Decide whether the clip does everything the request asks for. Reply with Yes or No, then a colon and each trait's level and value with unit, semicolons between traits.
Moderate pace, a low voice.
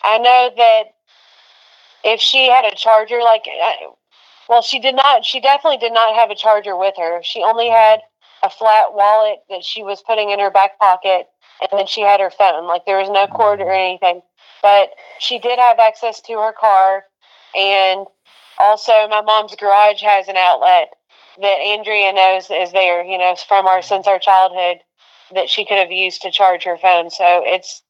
No: average, 190 wpm; high, 200 Hz